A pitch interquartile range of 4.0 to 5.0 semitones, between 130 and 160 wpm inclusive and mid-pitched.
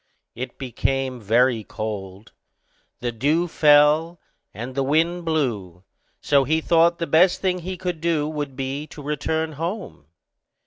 Yes: average, 4.7 semitones; average, 140 wpm; medium, 145 Hz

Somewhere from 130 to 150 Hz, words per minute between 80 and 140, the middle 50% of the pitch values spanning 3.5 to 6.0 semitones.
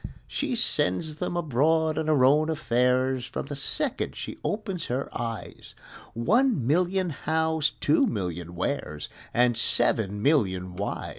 Yes: medium, 140 Hz; slow, 135 wpm; wide, 5.6 semitones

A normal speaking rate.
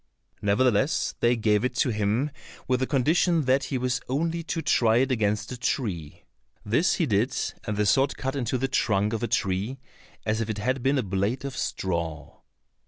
Yes: average, 195 wpm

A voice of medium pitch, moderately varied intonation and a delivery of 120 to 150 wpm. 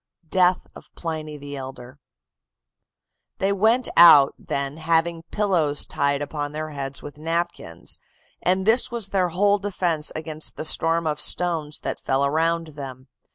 Yes: medium, 160 Hz; average, 3.6 semitones; average, 145 wpm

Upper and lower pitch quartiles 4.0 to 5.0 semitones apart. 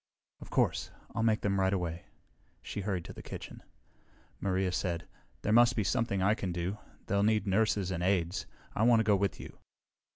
No: average, 2.7 semitones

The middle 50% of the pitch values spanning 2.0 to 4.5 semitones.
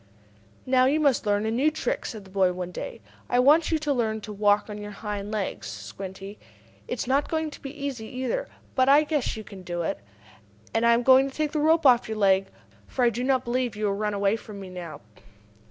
No: average, 5.0 semitones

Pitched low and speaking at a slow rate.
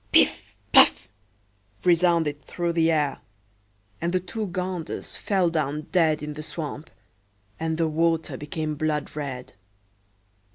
No: medium, 160 Hz; slow, 125 wpm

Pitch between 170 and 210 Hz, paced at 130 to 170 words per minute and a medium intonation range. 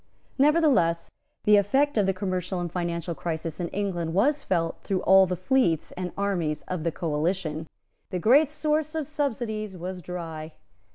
Yes: medium, 185 Hz; average, 160 wpm; average, 4.8 semitones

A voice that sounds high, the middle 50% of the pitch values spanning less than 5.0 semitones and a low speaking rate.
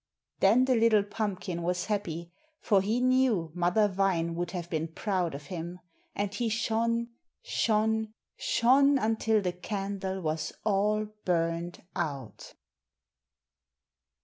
Yes: high, 195 Hz; average, 4.3 semitones; slow, 120 wpm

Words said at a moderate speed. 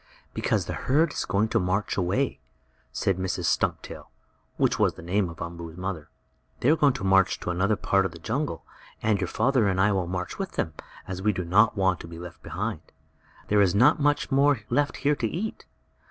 No: fast, 210 wpm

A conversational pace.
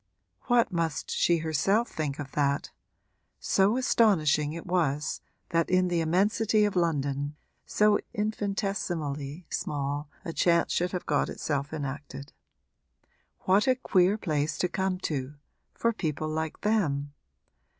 No: slow, 130 wpm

